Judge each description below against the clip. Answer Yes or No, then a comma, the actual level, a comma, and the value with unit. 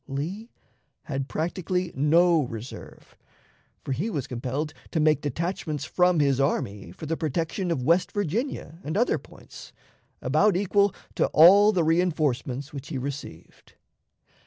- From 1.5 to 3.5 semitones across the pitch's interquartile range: No, average, 4.6 semitones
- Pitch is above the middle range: No, medium, 155 Hz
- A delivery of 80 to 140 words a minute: Yes, slow, 135 wpm